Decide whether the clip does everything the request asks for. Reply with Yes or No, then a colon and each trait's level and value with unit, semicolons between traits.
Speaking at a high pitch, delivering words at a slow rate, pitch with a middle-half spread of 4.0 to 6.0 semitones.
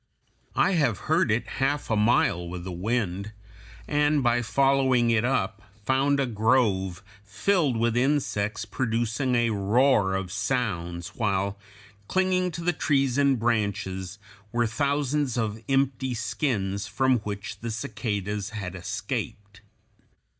No: low, 115 Hz; slow, 130 wpm; average, 4.8 semitones